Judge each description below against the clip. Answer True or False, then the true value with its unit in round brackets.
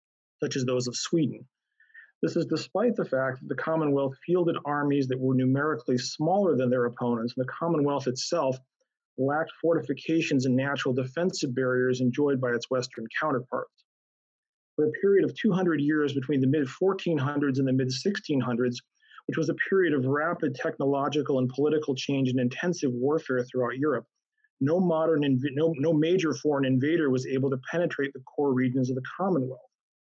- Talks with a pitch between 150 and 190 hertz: False (140 Hz)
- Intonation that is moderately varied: True (3.7 semitones)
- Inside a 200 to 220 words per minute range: False (165 wpm)